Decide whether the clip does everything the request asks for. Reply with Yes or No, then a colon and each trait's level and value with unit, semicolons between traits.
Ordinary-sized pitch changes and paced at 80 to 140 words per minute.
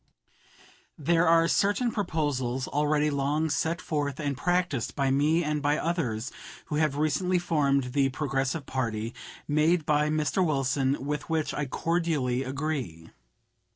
Yes: average, 3.0 semitones; slow, 135 wpm